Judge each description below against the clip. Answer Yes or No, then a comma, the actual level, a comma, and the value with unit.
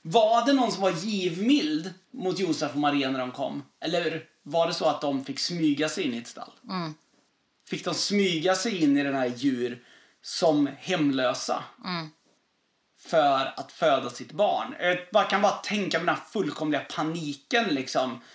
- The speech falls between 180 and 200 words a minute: No, average, 170 wpm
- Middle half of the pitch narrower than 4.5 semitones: No, average, 5.1 semitones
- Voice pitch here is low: No, medium, 165 Hz